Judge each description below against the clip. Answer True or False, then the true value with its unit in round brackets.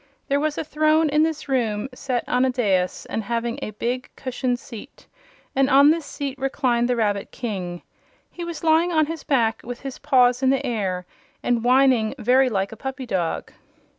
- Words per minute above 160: True (190 wpm)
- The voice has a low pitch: False (255 Hz)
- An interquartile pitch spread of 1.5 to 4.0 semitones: True (3.6 semitones)